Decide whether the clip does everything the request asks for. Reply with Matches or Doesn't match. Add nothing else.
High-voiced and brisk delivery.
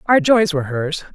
Matches